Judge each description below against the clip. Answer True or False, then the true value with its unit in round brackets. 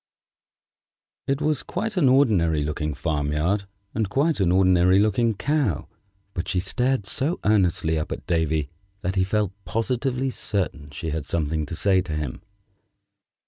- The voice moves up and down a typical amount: False (7.3 semitones)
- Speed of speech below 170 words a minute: True (150 wpm)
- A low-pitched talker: True (95 Hz)